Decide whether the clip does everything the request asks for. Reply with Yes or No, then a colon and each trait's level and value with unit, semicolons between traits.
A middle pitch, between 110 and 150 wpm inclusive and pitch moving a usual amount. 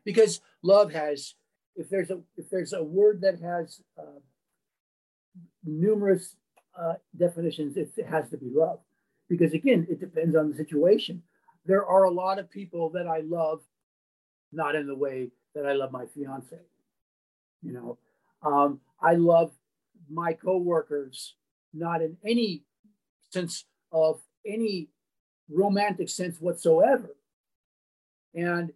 Yes: medium, 170 Hz; slow, 135 wpm; average, 4.1 semitones